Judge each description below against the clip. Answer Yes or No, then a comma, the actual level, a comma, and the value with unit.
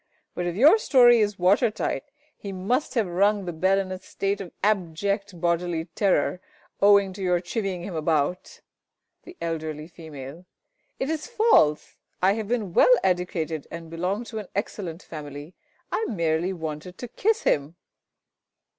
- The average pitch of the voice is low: No, medium, 185 Hz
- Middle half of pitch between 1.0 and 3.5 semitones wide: No, average, 3.9 semitones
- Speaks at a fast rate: No, average, 155 wpm